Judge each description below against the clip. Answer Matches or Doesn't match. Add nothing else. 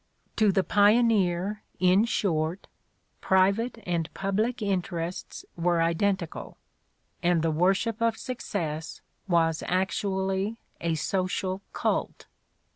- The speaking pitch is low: Doesn't match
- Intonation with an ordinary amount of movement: Matches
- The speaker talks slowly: Matches